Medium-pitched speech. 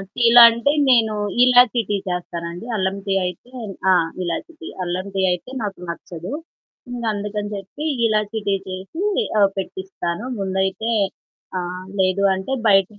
No: high, 200 Hz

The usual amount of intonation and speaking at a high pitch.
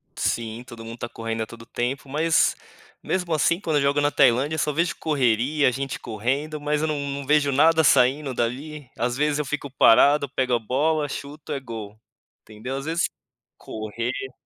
No: average, 3.9 semitones; medium, 140 Hz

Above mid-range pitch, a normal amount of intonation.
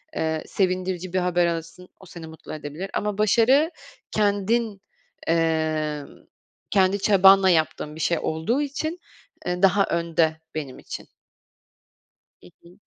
No: medium, 180 Hz; average, 3.9 semitones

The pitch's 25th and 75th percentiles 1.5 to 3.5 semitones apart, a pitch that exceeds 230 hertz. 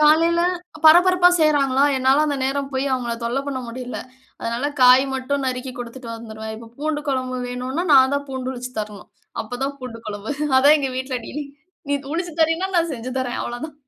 Yes: average, 2.9 semitones; very high, 265 Hz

